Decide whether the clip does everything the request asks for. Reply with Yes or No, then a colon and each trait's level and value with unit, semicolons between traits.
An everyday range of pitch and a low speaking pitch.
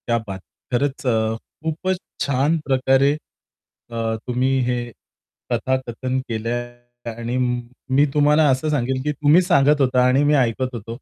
Yes: average, 3.0 semitones; low, 130 Hz